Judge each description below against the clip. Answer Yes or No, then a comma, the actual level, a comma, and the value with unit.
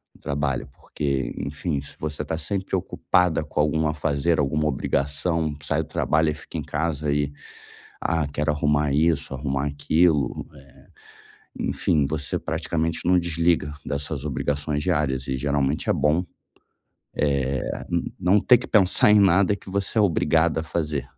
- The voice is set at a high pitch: No, very low, 75 Hz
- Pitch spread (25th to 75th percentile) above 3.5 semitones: No, average, 2.8 semitones